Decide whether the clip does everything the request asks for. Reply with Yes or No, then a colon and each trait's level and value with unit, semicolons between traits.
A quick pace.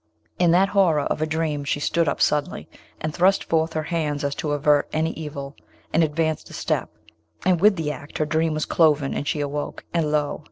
Yes: fast, 210 wpm